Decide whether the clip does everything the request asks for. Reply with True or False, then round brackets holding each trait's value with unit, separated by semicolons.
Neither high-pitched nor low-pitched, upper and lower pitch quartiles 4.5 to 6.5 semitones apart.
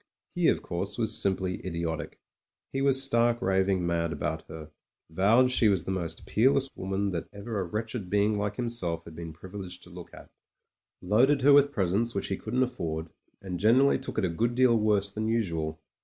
False (100 Hz; 5.2 semitones)